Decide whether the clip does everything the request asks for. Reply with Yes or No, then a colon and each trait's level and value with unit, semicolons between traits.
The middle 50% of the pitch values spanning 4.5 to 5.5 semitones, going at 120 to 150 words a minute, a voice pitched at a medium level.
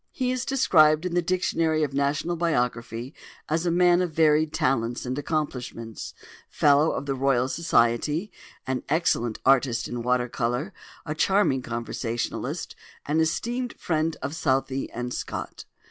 Yes: average, 5.1 semitones; average, 145 wpm; medium, 145 Hz